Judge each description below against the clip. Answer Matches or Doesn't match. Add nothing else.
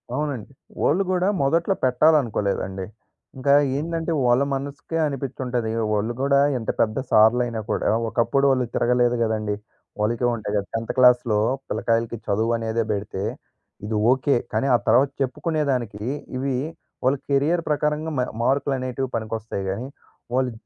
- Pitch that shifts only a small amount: Doesn't match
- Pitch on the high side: Doesn't match